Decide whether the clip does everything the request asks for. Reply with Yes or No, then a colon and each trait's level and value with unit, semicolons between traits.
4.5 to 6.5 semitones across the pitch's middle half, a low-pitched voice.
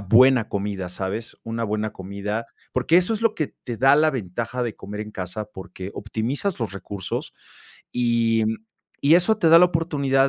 Yes: average, 5.2 semitones; low, 115 Hz